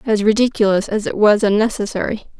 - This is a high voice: Yes, high, 215 Hz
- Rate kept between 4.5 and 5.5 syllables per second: No, 6.1 syllables/s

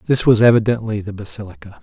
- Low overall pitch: Yes, low, 110 Hz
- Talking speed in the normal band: Yes, average, 165 wpm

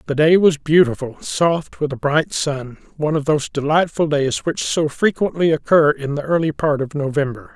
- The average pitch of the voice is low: No, medium, 150 Hz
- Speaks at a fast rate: No, average, 190 wpm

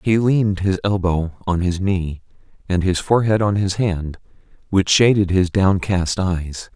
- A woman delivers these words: No, male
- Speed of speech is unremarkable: Yes, average, 160 wpm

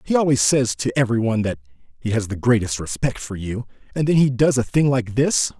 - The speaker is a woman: No, male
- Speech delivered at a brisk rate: Yes, fast, 235 wpm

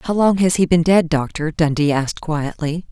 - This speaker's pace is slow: No, fast, 205 wpm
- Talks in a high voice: No, medium, 165 Hz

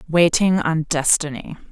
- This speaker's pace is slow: Yes, slow, 105 wpm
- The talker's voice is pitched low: No, medium, 160 Hz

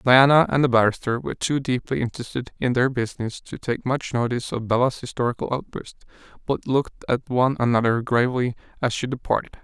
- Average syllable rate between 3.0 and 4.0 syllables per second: No, 6.1 syllables/s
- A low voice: Yes, low, 125 Hz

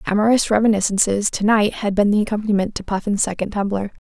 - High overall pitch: Yes, high, 210 Hz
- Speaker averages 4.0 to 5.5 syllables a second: No, 6.5 syllables/s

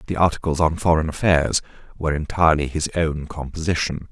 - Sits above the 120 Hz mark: No, very low, 80 Hz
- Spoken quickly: No, average, 145 wpm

